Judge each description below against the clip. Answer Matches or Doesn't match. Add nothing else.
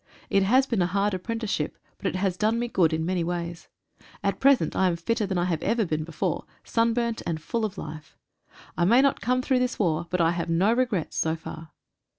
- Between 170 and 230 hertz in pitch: Matches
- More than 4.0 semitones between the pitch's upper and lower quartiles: Matches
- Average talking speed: Doesn't match